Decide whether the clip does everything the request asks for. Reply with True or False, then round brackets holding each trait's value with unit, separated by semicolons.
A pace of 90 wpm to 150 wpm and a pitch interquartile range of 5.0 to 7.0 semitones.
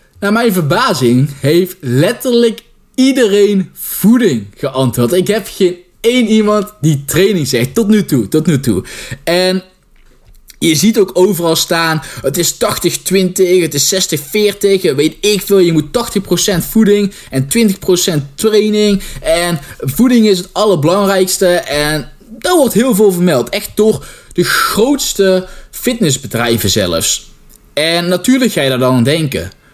True (140 wpm; 5.4 semitones)